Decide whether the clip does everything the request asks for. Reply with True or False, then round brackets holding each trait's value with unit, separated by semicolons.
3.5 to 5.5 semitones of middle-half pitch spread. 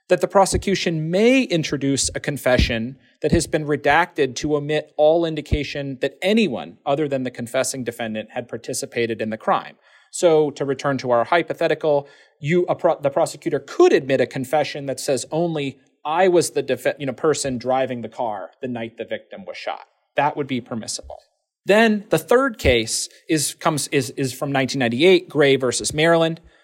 True (4.1 semitones)